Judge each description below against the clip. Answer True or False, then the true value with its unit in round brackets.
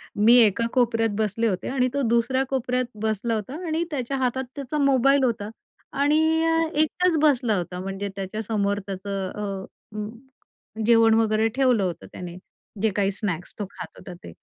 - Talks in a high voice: True (225 Hz)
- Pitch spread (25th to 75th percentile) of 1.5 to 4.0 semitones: False (4.5 semitones)